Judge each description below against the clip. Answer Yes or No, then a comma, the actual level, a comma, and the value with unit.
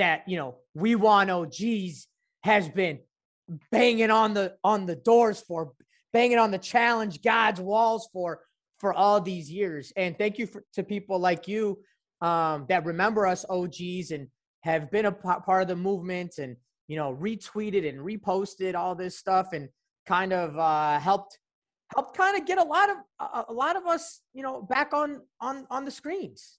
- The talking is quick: No, average, 185 wpm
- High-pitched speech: Yes, high, 195 Hz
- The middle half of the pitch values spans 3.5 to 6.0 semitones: Yes, average, 4.3 semitones